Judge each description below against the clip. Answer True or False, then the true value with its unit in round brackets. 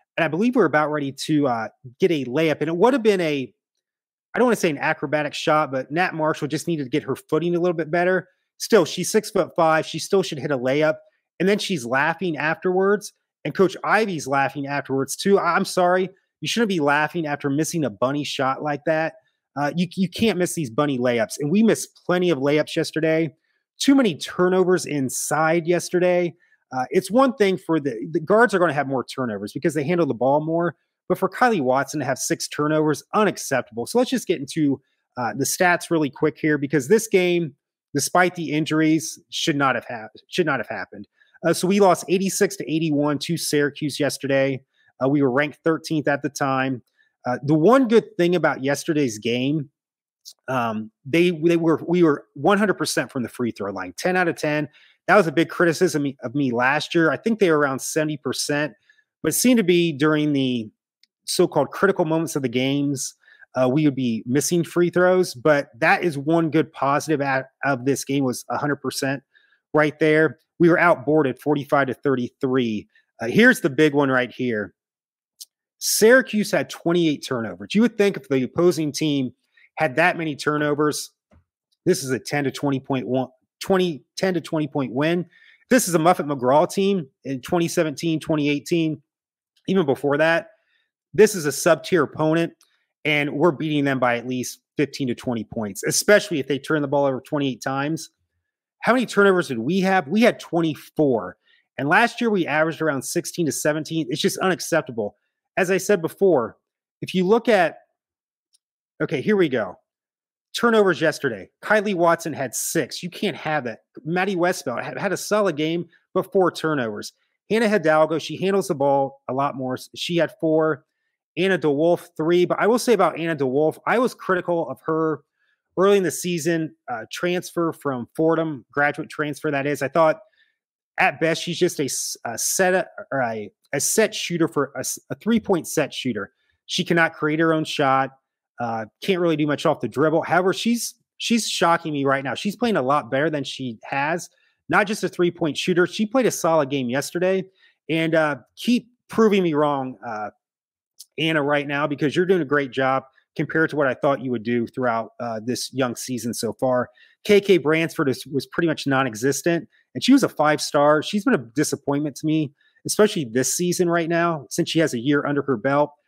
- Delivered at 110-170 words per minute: False (190 wpm)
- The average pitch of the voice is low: False (155 Hz)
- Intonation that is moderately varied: True (4.3 semitones)